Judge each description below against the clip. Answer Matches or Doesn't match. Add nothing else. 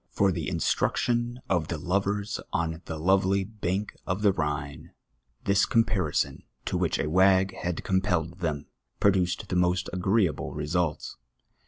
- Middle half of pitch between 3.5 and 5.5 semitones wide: Doesn't match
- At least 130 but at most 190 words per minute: Matches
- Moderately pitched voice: Doesn't match